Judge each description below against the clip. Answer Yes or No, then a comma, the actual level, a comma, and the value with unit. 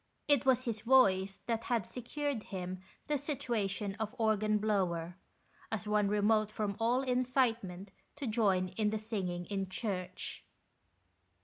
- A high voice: Yes, high, 215 Hz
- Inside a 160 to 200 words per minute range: No, slow, 135 wpm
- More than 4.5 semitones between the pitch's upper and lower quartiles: No, average, 3.6 semitones